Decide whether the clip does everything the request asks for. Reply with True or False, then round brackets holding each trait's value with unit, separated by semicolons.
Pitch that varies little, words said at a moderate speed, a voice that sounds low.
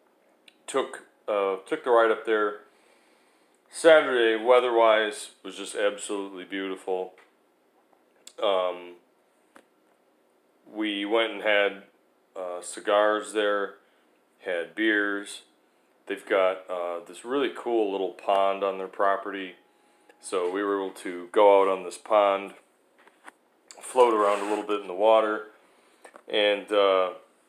False (2.3 semitones; 120 wpm; 100 Hz)